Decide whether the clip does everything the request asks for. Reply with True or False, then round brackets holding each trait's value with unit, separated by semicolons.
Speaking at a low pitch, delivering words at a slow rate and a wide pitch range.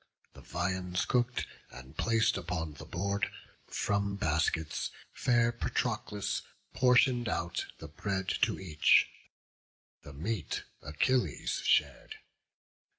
True (100 Hz; 100 wpm; 6.4 semitones)